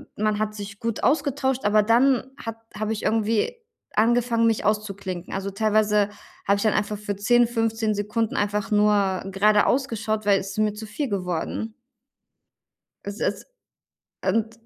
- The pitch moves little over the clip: Yes, narrow, 1.8 semitones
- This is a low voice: No, high, 215 Hz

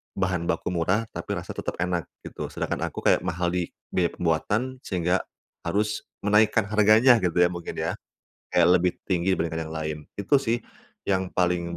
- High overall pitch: No, very low, 90 Hz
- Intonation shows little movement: No, average, 3.3 semitones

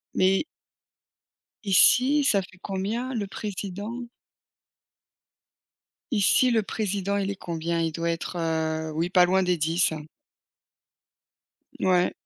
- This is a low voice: No, high, 190 Hz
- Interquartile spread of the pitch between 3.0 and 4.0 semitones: Yes, average, 3.5 semitones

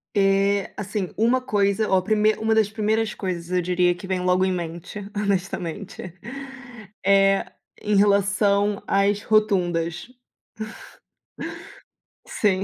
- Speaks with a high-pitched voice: Yes, high, 200 Hz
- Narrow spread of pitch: Yes, narrow, 2.3 semitones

